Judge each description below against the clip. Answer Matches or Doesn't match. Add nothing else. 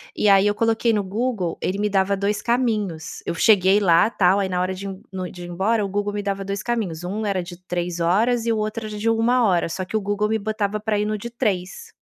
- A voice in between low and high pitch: Doesn't match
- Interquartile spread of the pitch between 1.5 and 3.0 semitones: Matches